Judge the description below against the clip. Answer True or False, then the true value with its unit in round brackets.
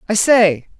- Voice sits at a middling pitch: False (200 Hz)